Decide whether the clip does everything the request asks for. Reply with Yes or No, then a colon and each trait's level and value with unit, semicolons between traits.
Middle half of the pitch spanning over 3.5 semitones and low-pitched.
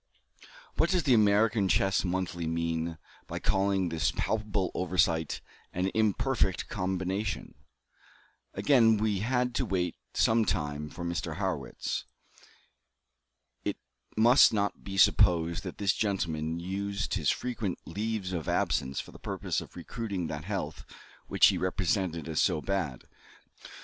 Yes: average, 4.0 semitones; very low, 95 Hz